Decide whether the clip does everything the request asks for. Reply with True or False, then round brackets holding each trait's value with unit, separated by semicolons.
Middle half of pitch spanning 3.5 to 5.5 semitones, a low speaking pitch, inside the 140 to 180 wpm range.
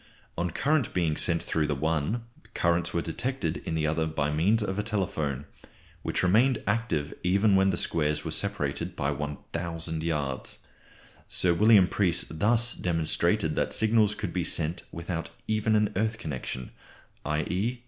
True (5.2 semitones; 85 Hz; 155 wpm)